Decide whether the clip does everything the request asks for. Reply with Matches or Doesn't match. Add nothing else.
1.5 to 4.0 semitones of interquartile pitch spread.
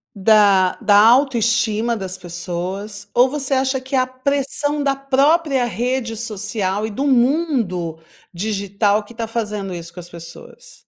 Doesn't match